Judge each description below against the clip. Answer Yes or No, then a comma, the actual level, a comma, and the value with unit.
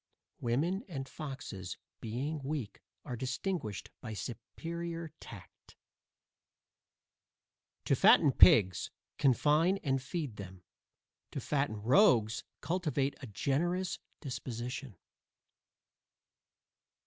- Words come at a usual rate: No, slow, 85 wpm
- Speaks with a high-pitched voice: No, low, 135 Hz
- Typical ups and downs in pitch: No, wide, 6.0 semitones